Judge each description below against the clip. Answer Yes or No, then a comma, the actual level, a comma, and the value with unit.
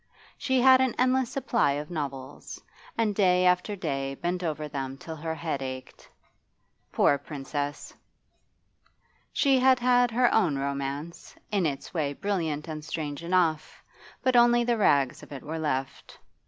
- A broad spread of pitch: Yes, wide, 7.7 semitones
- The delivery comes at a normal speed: Yes, average, 150 wpm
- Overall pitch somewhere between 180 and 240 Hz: No, medium, 160 Hz